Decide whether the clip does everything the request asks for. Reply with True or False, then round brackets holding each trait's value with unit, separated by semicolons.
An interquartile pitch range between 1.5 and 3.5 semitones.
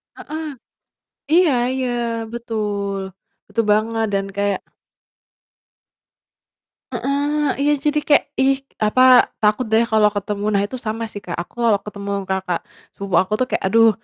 False (4.3 semitones)